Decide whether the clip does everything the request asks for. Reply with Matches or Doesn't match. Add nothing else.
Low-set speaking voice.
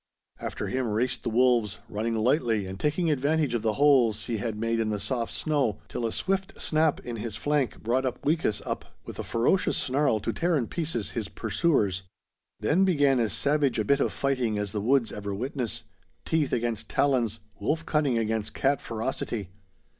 Matches